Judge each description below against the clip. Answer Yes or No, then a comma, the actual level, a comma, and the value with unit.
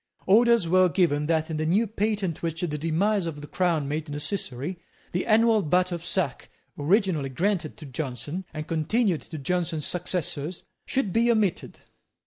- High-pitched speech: No, medium, 170 Hz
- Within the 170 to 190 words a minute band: No, average, 160 wpm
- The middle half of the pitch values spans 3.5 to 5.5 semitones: Yes, average, 4.2 semitones